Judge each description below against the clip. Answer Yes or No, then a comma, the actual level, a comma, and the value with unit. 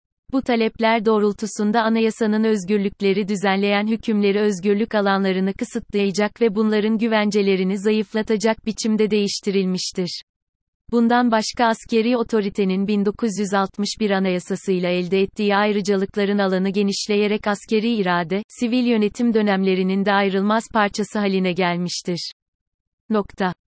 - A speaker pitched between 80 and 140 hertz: No, high, 205 Hz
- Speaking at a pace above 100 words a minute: No, slow, 95 wpm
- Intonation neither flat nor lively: No, narrow, 2.2 semitones